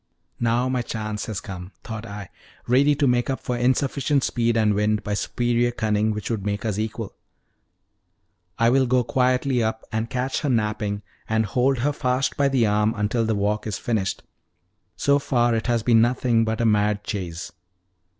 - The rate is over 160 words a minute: Yes, average, 180 wpm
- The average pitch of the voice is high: No, low, 115 Hz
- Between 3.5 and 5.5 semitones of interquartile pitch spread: No, average, 3.0 semitones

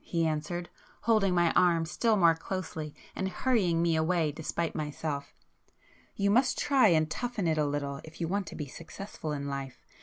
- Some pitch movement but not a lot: Yes, average, 3.7 semitones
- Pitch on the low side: No, medium, 165 Hz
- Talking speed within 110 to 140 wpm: No, average, 175 wpm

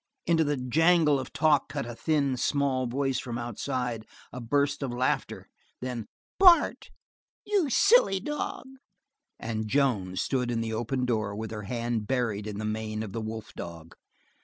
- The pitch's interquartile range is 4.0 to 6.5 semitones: Yes, average, 4.4 semitones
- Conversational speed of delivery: Yes, average, 160 wpm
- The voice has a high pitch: No, low, 125 Hz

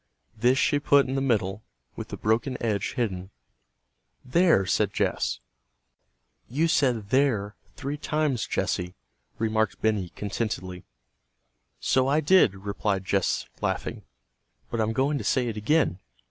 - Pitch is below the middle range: Yes, low, 115 Hz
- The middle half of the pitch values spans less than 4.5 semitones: No, average, 5.3 semitones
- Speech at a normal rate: No, slow, 130 wpm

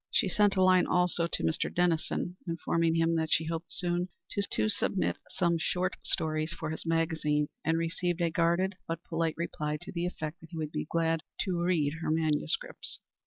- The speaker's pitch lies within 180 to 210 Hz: No, medium, 165 Hz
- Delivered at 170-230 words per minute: Yes, average, 185 wpm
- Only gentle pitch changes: Yes, narrow, 1.8 semitones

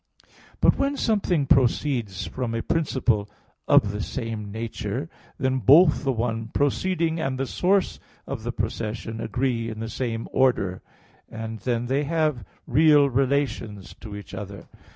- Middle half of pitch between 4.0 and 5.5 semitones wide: Yes, average, 4.3 semitones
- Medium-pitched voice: No, low, 125 Hz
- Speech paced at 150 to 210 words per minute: No, average, 140 wpm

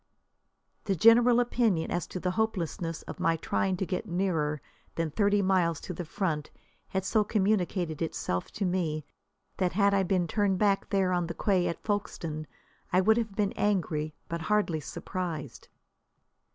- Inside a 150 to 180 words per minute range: Yes, average, 165 wpm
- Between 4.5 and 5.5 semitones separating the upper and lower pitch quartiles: No, average, 3.5 semitones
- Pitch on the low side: No, medium, 185 Hz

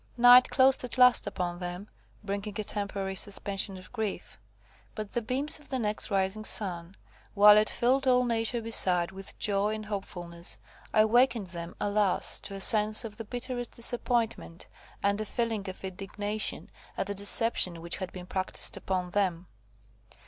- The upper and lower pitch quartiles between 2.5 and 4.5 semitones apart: Yes, average, 3.4 semitones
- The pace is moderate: Yes, average, 160 wpm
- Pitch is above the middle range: Yes, high, 205 Hz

